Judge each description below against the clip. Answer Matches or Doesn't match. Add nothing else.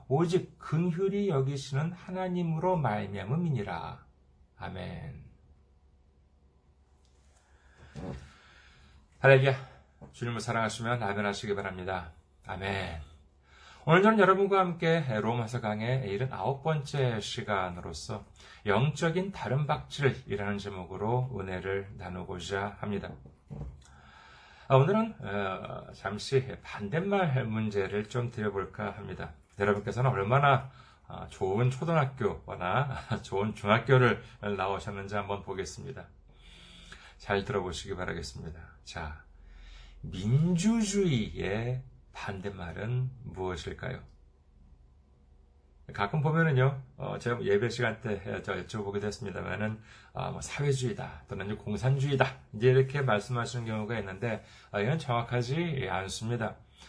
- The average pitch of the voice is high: Doesn't match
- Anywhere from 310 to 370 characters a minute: Doesn't match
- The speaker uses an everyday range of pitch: Doesn't match